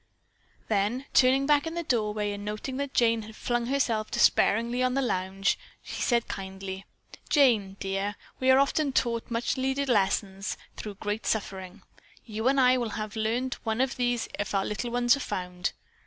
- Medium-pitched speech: No, high, 230 Hz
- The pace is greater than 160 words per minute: Yes, average, 180 wpm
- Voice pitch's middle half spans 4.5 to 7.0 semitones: No, average, 3.9 semitones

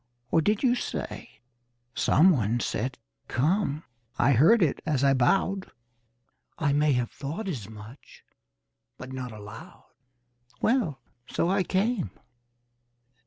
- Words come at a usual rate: No, slow, 120 wpm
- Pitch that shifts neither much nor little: No, wide, 7.3 semitones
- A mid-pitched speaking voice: Yes, medium, 145 Hz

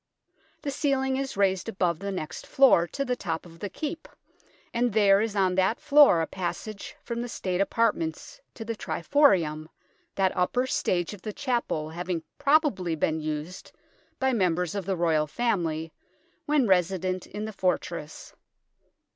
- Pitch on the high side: Yes, high, 195 Hz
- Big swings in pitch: Yes, wide, 5.8 semitones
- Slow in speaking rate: No, average, 155 wpm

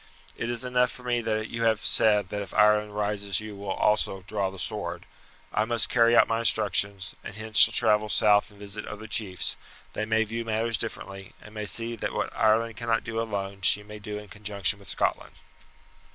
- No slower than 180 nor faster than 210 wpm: Yes, fast, 205 wpm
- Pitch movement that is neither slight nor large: No, narrow, 1.8 semitones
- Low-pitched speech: Yes, low, 105 Hz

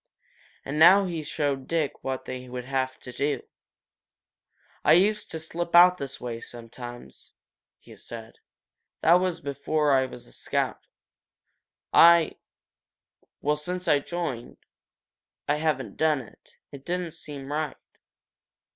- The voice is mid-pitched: Yes, medium, 145 Hz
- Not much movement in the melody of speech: No, average, 4.3 semitones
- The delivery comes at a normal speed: No, slow, 130 wpm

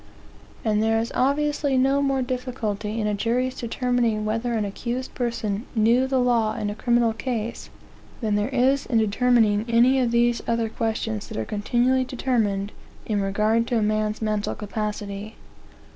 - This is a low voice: No, high, 230 Hz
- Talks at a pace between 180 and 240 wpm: No, average, 160 wpm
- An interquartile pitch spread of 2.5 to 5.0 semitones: Yes, average, 2.8 semitones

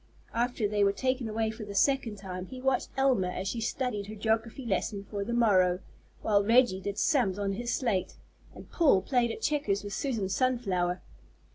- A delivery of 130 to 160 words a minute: No, average, 185 wpm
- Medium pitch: No, high, 220 Hz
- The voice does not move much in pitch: No, average, 3.9 semitones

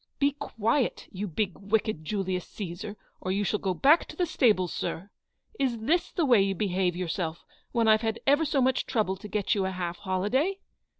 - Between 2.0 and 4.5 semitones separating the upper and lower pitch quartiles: No, average, 5.1 semitones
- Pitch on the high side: Yes, high, 205 Hz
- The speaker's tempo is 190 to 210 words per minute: Yes, average, 200 wpm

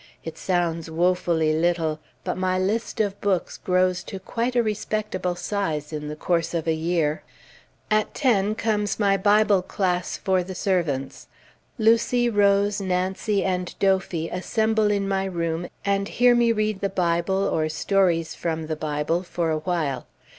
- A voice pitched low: No, medium, 185 Hz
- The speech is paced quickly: No, average, 155 wpm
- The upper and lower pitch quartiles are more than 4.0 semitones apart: No, average, 3.5 semitones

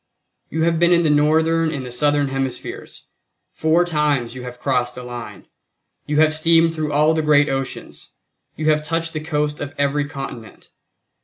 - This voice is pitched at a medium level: Yes, medium, 150 Hz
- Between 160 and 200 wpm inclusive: Yes, average, 175 wpm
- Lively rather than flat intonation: No, average, 2.9 semitones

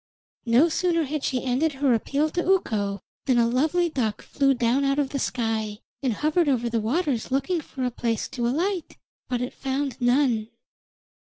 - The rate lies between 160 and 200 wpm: Yes, average, 180 wpm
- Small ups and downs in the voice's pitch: No, average, 4.2 semitones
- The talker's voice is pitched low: No, very high, 265 Hz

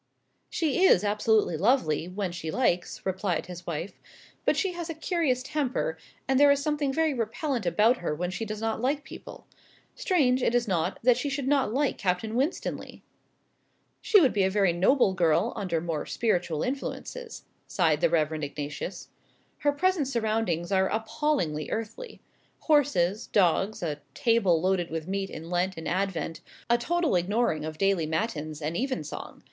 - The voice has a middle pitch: No, high, 205 Hz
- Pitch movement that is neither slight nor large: No, wide, 7.5 semitones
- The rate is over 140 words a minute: Yes, average, 165 wpm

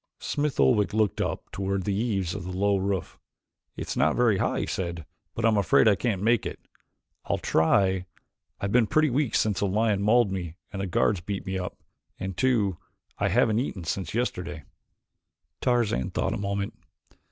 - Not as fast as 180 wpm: No, average, 185 wpm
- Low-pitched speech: Yes, low, 100 Hz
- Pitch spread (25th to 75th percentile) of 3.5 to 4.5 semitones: No, average, 3.1 semitones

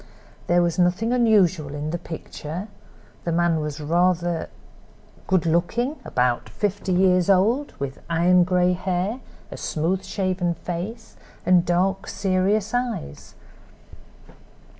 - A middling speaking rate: No, slow, 120 wpm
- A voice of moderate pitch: Yes, medium, 180 Hz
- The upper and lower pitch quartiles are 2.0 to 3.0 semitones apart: Yes, narrow, 2.4 semitones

